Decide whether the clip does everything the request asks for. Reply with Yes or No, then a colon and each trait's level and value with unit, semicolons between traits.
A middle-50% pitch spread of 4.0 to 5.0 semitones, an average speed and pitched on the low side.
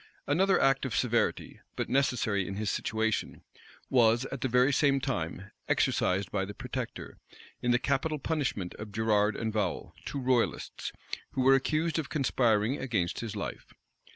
Yes: average, 4.5 semitones; average, 155 wpm; low, 120 Hz